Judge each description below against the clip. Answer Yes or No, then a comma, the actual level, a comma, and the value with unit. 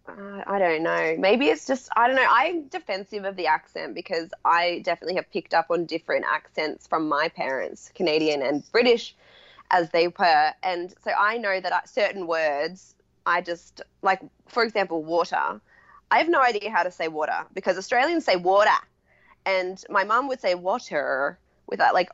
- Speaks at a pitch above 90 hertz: Yes, high, 190 Hz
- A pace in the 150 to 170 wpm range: No, average, 180 wpm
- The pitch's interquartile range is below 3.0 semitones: No, average, 5.2 semitones